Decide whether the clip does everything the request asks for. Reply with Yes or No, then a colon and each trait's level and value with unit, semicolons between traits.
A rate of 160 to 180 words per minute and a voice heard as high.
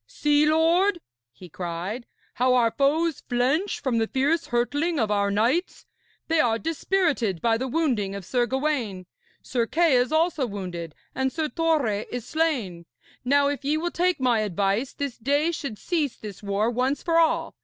Yes: average, 170 wpm; very high, 260 Hz